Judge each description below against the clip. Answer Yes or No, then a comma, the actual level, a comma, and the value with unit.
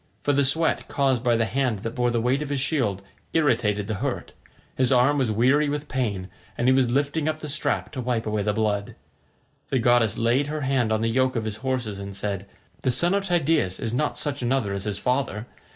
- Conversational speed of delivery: No, fast, 225 wpm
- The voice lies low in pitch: Yes, low, 125 Hz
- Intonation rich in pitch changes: No, average, 4.3 semitones